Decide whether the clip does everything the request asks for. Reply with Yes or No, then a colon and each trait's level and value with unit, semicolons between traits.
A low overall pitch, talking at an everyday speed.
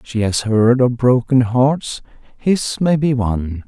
Yes: low, 125 Hz; average, 165 wpm